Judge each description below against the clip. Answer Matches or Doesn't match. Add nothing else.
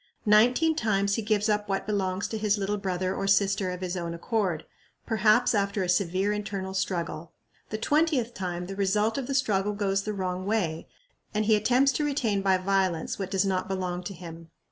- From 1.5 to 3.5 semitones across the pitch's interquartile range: Matches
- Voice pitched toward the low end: Doesn't match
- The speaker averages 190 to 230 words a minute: Matches